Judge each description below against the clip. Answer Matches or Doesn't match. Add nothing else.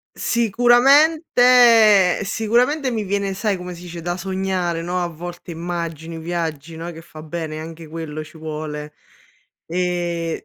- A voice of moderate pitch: Matches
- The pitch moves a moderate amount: Matches